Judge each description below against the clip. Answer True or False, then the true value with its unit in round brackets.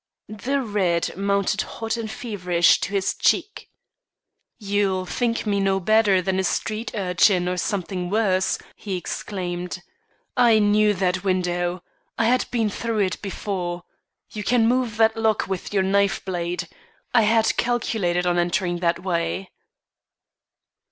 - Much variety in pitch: False (3.3 semitones)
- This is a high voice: True (195 Hz)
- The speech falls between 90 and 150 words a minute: True (140 wpm)